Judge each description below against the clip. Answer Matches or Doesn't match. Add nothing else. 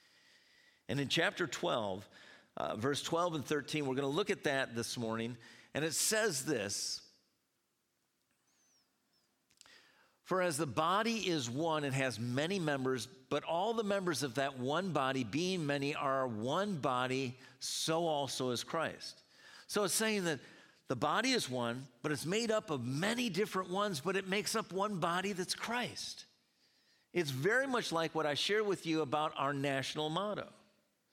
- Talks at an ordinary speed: Matches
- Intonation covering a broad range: Matches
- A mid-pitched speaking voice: Matches